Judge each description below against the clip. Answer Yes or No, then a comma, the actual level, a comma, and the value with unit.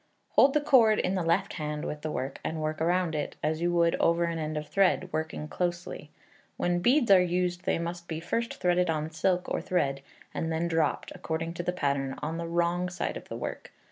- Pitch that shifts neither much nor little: No, narrow, 2.3 semitones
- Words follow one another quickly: Yes, fast, 220 wpm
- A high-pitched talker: No, medium, 170 Hz